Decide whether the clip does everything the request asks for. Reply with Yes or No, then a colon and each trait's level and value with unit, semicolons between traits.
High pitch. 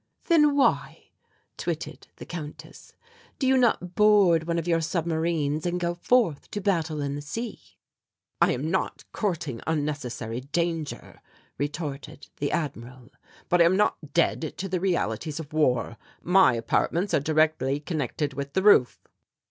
No: medium, 160 Hz